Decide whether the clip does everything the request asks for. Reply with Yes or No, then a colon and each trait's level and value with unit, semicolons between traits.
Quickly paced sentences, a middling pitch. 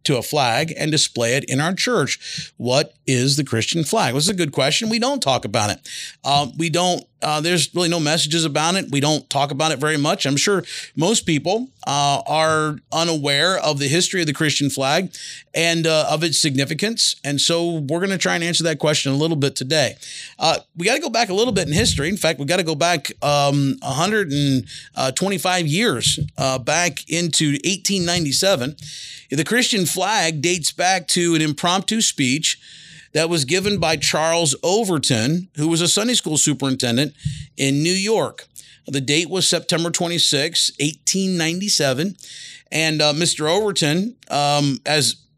No: average, 180 wpm; medium, 160 Hz